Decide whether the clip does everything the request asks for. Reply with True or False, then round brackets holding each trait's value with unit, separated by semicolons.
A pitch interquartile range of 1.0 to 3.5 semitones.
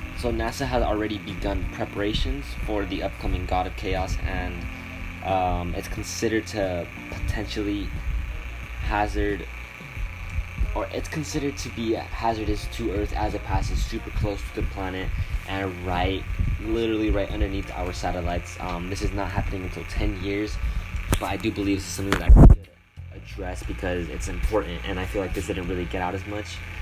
True (2.7 semitones)